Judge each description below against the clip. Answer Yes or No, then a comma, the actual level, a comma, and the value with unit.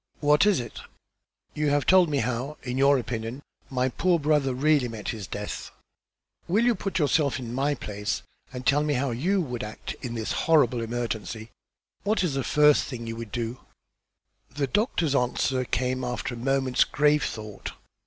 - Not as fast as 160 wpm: No, average, 175 wpm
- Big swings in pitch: No, average, 3.8 semitones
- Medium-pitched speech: No, low, 130 Hz